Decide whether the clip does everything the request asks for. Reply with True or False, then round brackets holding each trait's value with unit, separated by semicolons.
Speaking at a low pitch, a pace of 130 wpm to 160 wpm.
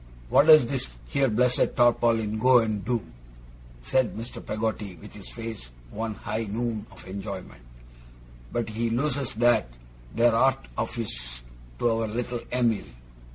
True (115 Hz; 145 wpm)